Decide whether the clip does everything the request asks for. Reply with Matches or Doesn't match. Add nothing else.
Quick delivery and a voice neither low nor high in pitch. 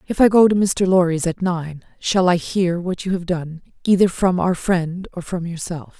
Matches